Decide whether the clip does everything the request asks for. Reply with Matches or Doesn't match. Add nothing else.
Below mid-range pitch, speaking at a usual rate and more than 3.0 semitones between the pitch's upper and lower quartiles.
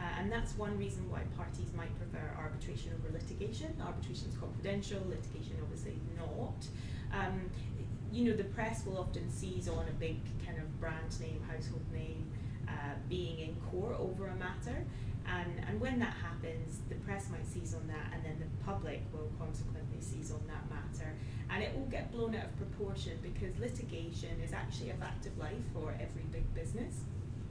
Doesn't match